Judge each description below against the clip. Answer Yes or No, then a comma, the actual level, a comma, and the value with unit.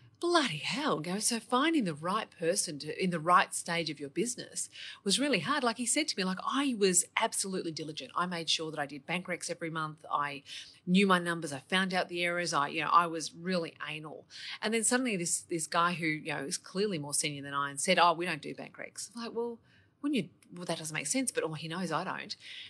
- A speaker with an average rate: No, fast, 245 wpm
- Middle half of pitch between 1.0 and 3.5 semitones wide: No, average, 4.6 semitones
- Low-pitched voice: No, medium, 175 Hz